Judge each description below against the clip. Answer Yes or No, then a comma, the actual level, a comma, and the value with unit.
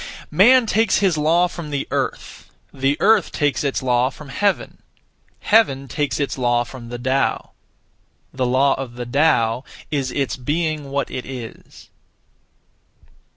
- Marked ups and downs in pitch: No, average, 3.8 semitones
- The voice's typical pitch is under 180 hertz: Yes, medium, 140 Hz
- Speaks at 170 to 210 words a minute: No, average, 145 wpm